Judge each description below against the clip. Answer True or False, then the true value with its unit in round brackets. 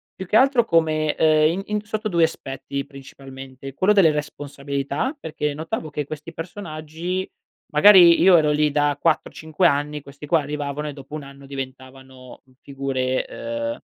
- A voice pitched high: False (150 Hz)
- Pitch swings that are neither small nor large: True (3.2 semitones)